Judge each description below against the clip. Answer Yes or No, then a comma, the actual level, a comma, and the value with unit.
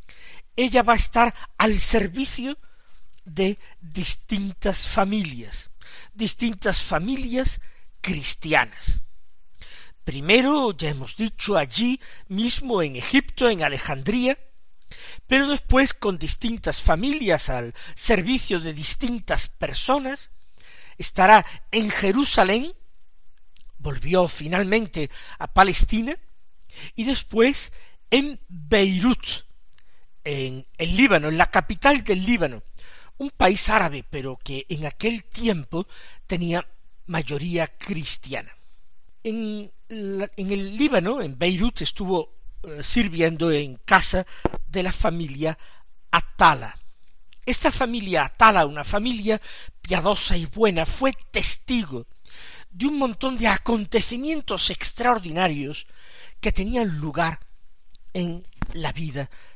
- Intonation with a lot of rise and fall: Yes, wide, 6.7 semitones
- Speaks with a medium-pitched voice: No, high, 200 Hz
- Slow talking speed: Yes, slow, 100 wpm